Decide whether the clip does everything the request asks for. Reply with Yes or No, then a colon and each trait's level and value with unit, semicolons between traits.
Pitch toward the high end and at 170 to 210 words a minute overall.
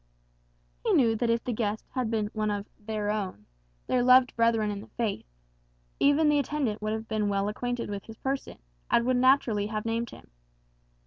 Yes: high, 225 Hz; average, 190 wpm